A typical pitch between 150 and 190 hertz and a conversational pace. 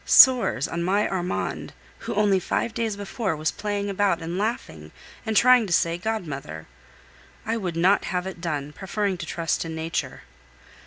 Yes: medium, 185 Hz; average, 165 wpm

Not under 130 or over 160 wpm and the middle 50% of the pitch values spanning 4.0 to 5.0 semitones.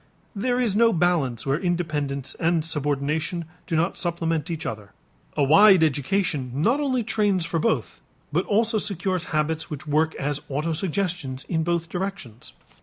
Yes: average, 150 wpm; average, 4.3 semitones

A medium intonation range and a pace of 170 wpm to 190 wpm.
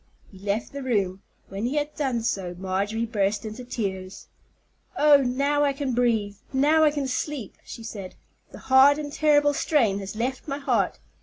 No: wide, 6.0 semitones; average, 175 wpm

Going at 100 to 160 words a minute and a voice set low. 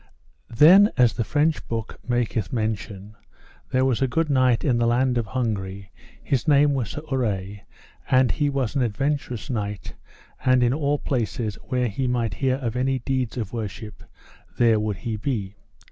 No: average, 170 wpm; low, 120 Hz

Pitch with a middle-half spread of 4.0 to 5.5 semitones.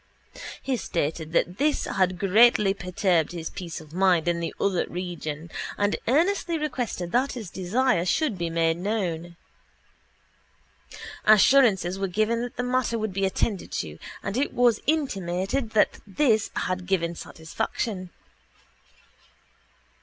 Yes: average, 5.2 semitones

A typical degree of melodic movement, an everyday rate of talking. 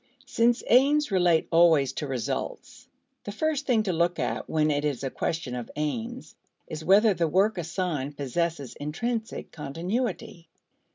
No: wide, 6.6 semitones; average, 150 wpm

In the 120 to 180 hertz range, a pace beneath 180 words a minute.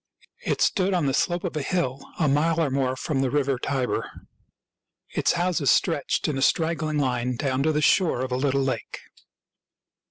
No: medium, 140 Hz; average, 185 wpm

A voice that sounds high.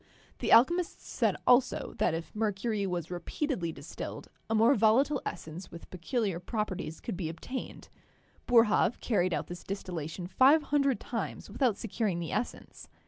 Yes: high, 210 Hz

